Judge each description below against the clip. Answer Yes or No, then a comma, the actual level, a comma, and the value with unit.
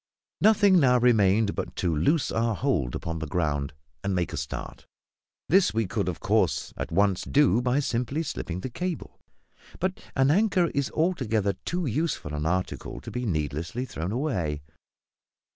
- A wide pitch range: Yes, wide, 9.0 semitones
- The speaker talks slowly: No, average, 160 wpm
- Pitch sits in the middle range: No, low, 115 Hz